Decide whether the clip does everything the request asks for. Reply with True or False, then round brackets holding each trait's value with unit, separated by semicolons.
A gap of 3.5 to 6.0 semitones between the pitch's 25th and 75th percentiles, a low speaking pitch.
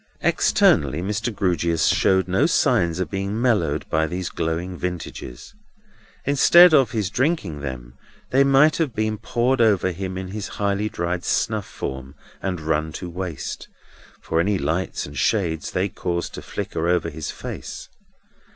True (4.7 semitones; 95 Hz)